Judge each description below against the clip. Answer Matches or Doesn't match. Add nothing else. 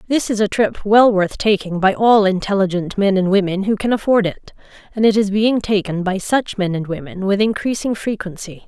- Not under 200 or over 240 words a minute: Matches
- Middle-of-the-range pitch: Doesn't match